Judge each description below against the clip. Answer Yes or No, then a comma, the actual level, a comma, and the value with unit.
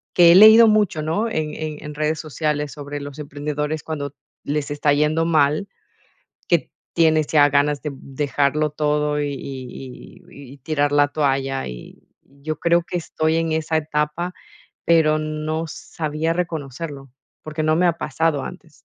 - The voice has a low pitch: No, medium, 150 Hz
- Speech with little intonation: Yes, narrow, 1.7 semitones